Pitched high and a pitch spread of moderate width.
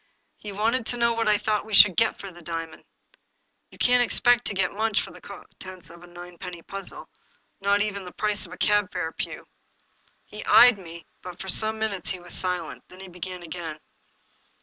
Yes: high, 195 Hz; average, 3.4 semitones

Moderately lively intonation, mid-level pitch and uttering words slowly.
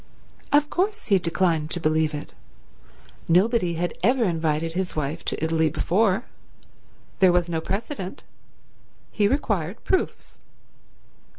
Yes: average, 5.0 semitones; medium, 175 Hz; slow, 120 wpm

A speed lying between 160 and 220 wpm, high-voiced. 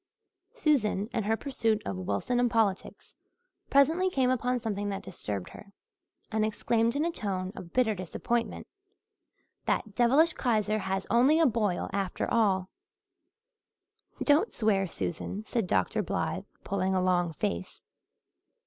No: slow, 135 wpm; high, 215 Hz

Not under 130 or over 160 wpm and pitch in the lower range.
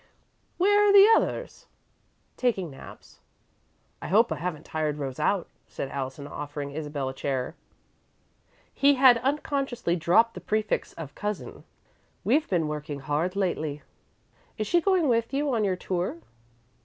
No: average, 145 wpm; medium, 180 Hz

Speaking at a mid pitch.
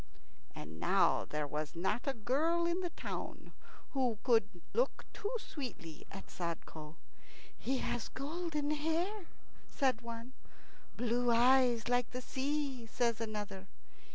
No: high, 245 Hz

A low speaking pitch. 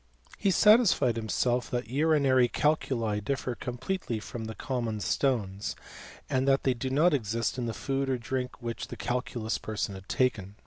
Yes: low, 125 Hz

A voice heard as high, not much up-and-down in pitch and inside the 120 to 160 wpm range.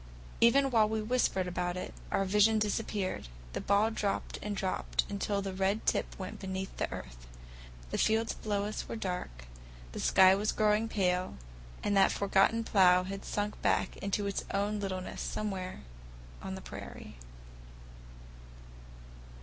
Yes: high, 200 Hz; narrow, 2.2 semitones; average, 150 wpm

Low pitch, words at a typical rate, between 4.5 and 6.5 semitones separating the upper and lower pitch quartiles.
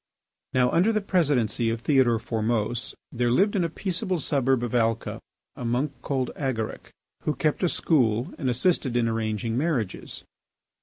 Yes: low, 125 Hz; average, 155 wpm; average, 4.9 semitones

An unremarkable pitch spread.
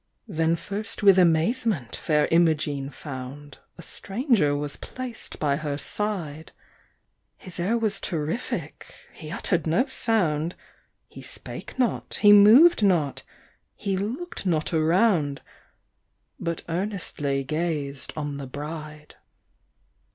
No: wide, 5.7 semitones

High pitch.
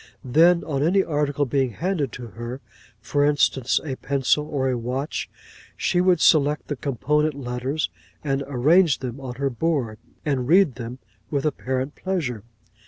No: medium, 140 Hz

